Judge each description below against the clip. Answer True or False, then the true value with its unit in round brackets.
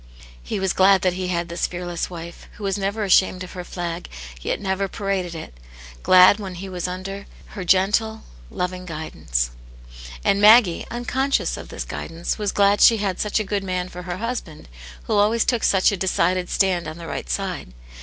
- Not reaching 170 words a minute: False (190 wpm)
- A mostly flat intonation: True (2.3 semitones)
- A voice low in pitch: False (185 Hz)